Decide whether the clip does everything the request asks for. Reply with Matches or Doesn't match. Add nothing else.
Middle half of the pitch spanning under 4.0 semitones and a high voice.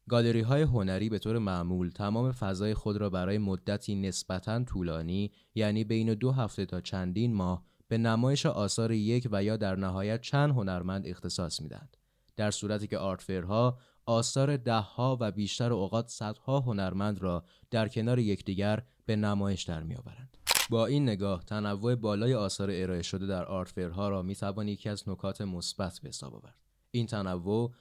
Doesn't match